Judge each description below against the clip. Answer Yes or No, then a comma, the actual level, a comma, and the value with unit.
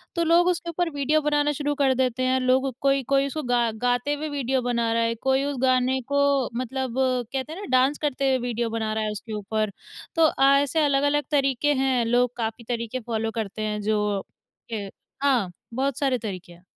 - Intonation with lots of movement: No, average, 3.5 semitones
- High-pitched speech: Yes, very high, 260 Hz